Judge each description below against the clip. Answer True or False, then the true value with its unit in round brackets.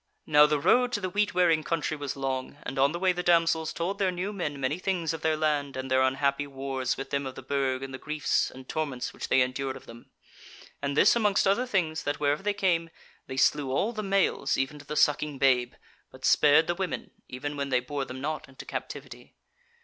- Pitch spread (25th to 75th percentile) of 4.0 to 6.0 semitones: True (4.3 semitones)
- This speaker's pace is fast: True (225 wpm)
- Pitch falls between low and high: True (145 Hz)